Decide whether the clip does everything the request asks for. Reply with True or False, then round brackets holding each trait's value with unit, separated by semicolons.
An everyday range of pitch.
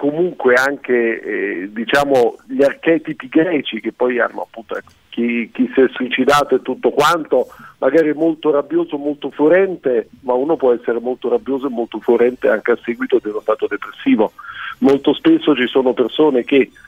True (4.6 semitones)